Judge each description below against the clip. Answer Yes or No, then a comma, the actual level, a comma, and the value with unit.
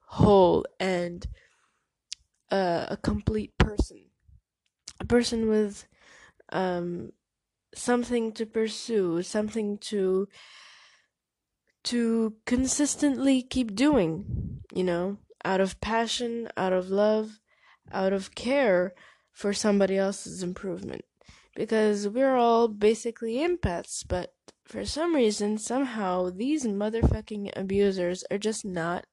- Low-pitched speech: No, high, 210 Hz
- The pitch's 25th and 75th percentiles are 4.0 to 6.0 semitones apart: No, average, 3.6 semitones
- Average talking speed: No, slow, 105 wpm